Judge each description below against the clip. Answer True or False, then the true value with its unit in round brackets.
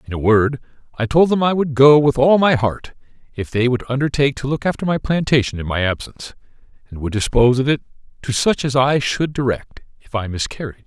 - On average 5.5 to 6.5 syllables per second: True (5.8 syllables/s)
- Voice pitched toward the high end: False (130 Hz)